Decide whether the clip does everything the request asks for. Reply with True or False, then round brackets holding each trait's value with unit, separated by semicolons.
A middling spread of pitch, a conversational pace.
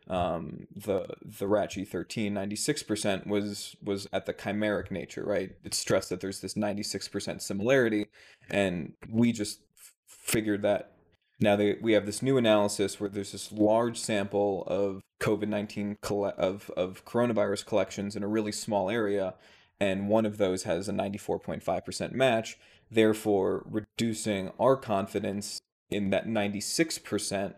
False (1.6 semitones; 145 wpm)